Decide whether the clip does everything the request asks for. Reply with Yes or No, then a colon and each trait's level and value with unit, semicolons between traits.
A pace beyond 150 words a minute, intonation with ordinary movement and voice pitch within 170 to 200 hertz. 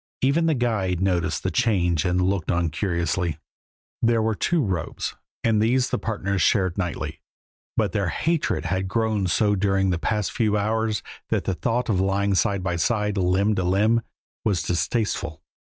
No: average, 170 wpm; average, 3.6 semitones; low, 100 Hz